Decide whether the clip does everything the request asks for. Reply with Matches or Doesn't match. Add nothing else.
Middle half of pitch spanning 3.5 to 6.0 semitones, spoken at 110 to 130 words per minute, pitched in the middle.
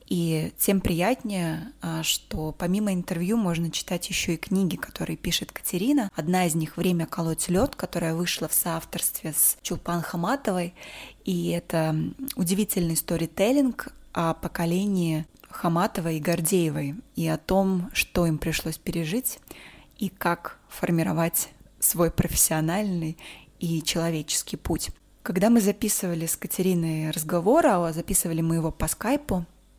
Doesn't match